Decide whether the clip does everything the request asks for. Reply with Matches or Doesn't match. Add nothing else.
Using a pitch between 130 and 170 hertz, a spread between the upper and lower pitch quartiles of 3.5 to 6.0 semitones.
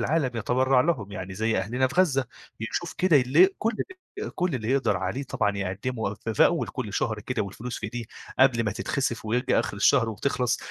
Doesn't match